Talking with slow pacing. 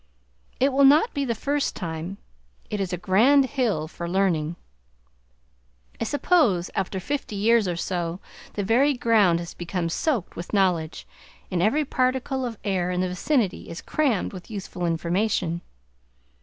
No: average, 155 wpm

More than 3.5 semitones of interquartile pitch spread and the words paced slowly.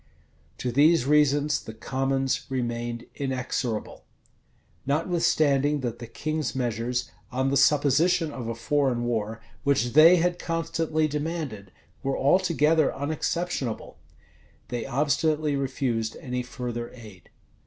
Yes: average, 4.2 semitones; slow, 115 wpm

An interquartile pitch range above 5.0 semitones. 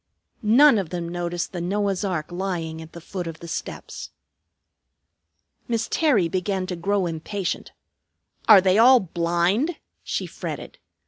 No: average, 3.3 semitones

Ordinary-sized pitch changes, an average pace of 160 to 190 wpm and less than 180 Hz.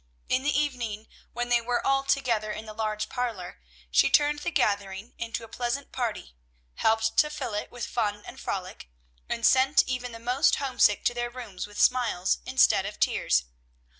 No: average, 3.2 semitones; average, 180 wpm; high, 235 Hz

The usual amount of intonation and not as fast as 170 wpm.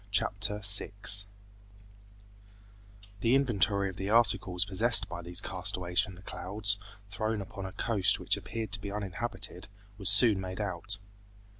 No: narrow, 2.1 semitones; average, 140 wpm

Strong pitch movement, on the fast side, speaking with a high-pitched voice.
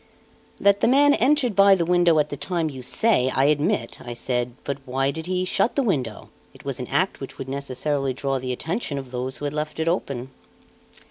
No: wide, 5.8 semitones; fast, 215 wpm; medium, 145 Hz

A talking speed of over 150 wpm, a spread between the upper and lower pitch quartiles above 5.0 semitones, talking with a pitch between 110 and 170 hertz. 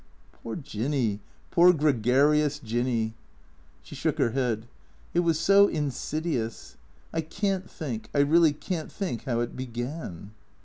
No: average, 140 wpm; wide, 5.5 semitones; medium, 140 Hz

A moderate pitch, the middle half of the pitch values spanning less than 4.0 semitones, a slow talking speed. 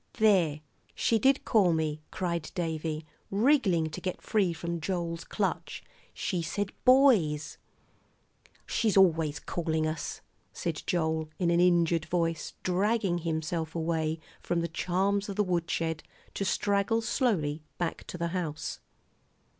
Yes: medium, 170 Hz; average, 3.5 semitones; slow, 130 wpm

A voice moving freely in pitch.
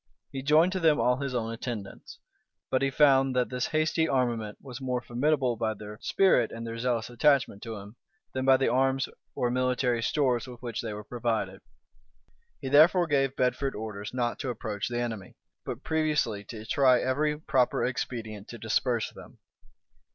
No: average, 3.0 semitones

